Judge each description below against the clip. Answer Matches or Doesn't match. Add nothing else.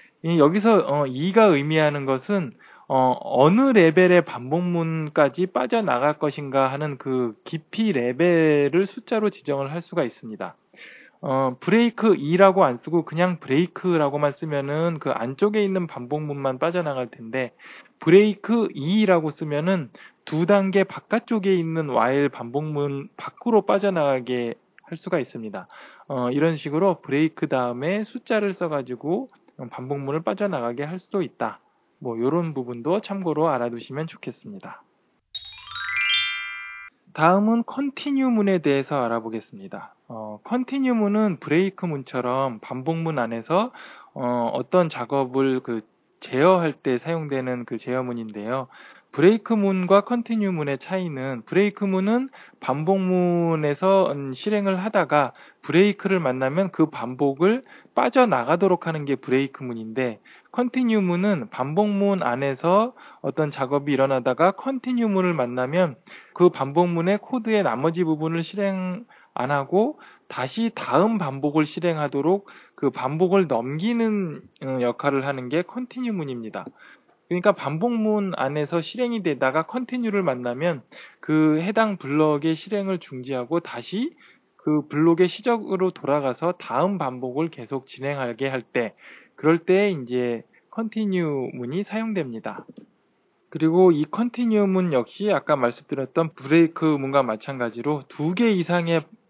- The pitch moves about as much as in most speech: Doesn't match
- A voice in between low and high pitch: Matches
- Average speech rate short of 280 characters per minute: Doesn't match